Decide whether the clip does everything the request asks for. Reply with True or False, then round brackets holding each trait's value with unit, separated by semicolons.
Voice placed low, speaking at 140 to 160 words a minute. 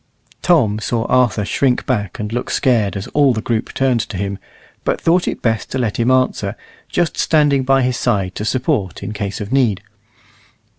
False (120 Hz; 190 wpm)